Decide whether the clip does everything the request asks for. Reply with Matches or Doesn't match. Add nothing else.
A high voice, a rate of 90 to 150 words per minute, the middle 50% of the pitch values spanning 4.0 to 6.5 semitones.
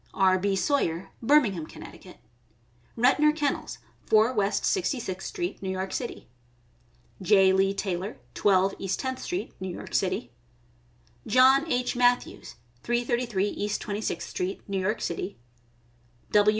Matches